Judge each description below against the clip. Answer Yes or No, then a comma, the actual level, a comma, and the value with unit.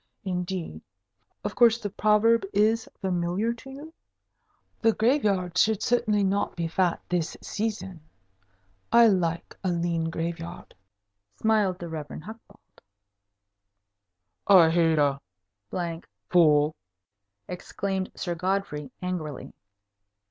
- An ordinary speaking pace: No, slow, 105 wpm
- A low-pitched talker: No, medium, 185 Hz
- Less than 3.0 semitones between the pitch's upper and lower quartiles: No, average, 4.2 semitones